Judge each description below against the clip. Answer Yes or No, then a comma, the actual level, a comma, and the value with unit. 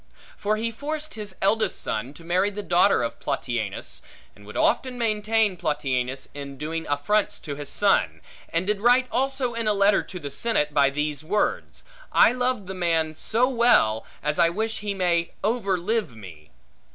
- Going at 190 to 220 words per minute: No, average, 175 wpm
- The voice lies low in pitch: No, medium, 185 Hz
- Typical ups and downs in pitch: No, wide, 7.2 semitones